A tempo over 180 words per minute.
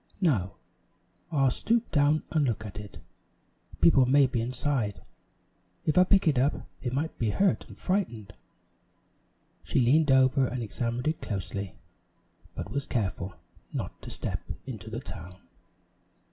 No: average, 145 wpm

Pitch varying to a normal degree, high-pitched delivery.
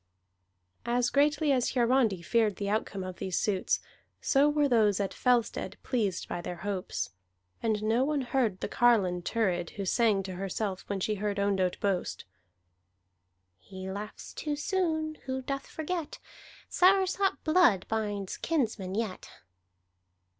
No: wide, 6.0 semitones; high, 220 Hz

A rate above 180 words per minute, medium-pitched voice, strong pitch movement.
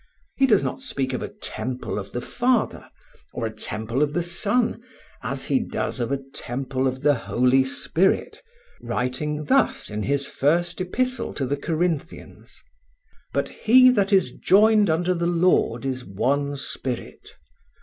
No: average, 155 wpm; medium, 145 Hz; wide, 6.7 semitones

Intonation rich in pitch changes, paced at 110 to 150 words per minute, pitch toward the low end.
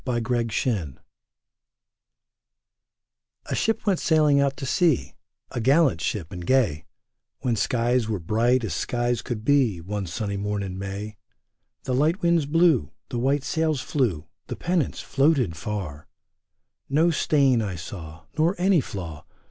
Yes: wide, 6.6 semitones; average, 145 wpm; low, 120 Hz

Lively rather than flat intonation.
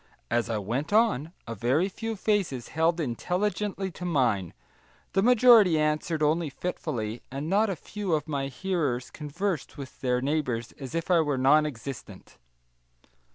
Yes: wide, 6.3 semitones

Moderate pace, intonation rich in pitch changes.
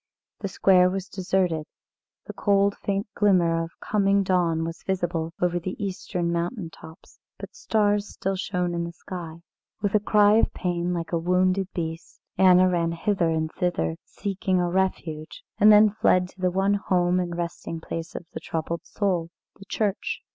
No: average, 170 wpm; average, 2.7 semitones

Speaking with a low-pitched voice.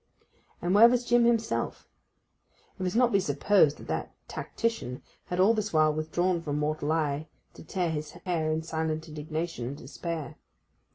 No: medium, 160 Hz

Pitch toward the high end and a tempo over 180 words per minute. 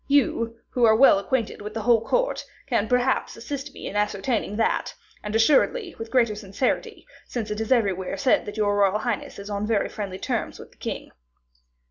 Yes: high, 225 Hz; average, 190 wpm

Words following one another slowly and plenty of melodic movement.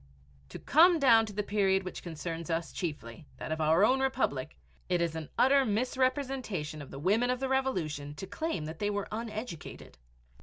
No: average, 185 wpm; wide, 8.0 semitones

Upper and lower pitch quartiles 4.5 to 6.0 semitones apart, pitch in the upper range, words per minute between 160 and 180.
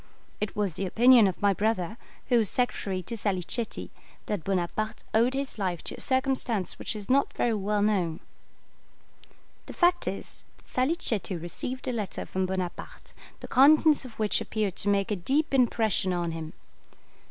Yes: average, 5.0 semitones; high, 210 Hz; average, 165 wpm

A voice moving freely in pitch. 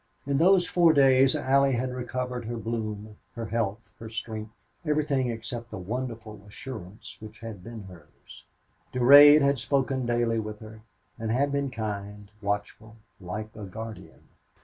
No: average, 3.5 semitones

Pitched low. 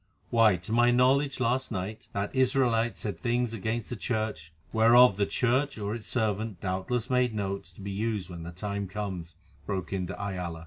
Yes: low, 110 Hz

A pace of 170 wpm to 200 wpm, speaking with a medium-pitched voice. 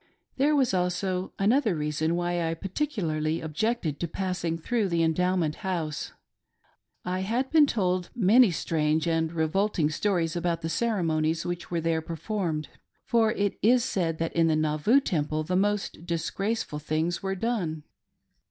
No: average, 150 wpm; medium, 175 Hz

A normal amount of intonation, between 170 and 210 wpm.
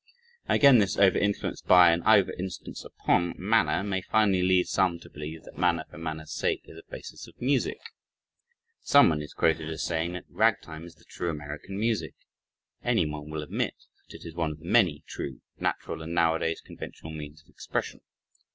Yes: average, 3.5 semitones; average, 180 wpm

